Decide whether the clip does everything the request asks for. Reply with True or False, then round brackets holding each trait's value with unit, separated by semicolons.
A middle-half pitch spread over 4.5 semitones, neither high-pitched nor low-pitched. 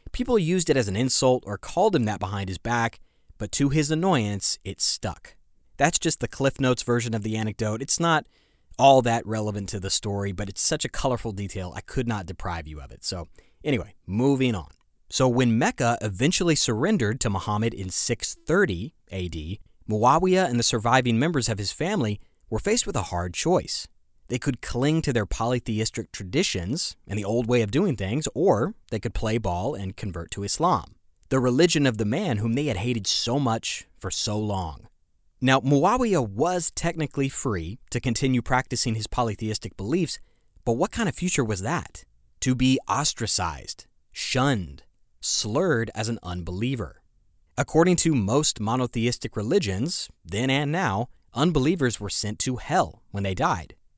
False (4.9 semitones; 115 Hz)